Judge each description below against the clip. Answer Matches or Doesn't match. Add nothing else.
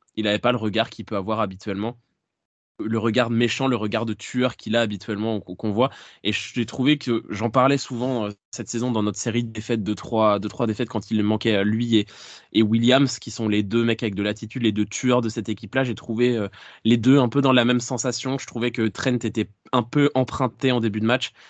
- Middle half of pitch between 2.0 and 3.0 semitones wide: Matches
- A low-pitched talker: Matches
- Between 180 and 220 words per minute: Doesn't match